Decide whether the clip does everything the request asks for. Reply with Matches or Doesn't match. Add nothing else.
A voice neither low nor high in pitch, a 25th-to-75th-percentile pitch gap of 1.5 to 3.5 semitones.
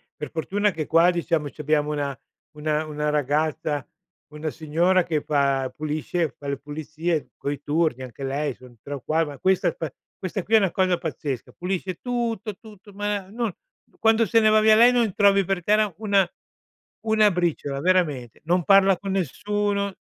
Doesn't match